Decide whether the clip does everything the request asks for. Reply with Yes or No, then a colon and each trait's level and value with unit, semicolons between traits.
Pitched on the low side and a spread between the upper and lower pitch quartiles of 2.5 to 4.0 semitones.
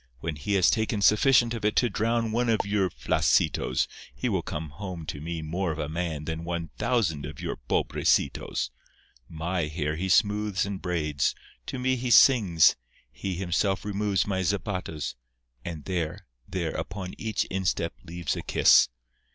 No: very low, 95 Hz; average, 4.4 semitones